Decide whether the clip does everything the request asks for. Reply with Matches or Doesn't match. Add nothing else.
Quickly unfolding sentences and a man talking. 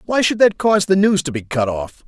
Matches